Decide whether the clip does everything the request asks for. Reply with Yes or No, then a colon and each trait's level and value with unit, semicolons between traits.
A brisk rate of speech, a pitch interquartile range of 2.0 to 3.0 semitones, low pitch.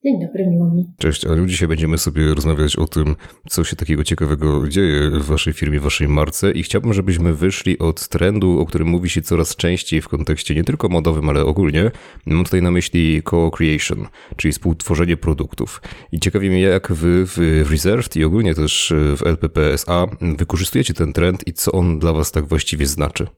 Yes: fast, 180 wpm; average, 2.7 semitones; very low, 85 Hz